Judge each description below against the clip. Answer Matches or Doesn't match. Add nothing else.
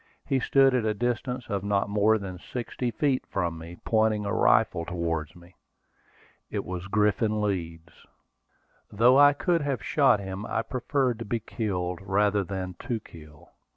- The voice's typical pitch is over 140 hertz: Doesn't match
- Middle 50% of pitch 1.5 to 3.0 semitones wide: Doesn't match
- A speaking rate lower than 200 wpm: Matches